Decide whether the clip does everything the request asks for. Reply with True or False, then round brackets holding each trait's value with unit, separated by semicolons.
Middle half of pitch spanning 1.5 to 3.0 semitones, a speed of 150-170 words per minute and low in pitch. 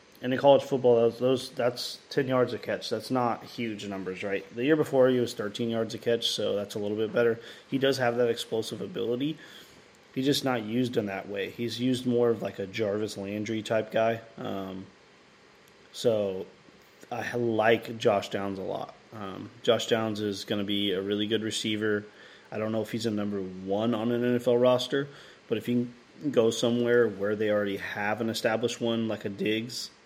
False (2.5 semitones; 200 wpm; 115 Hz)